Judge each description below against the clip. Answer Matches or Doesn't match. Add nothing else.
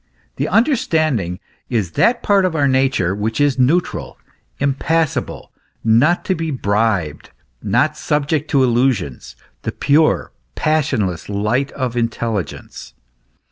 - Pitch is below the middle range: Matches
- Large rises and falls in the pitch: Matches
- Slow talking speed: Matches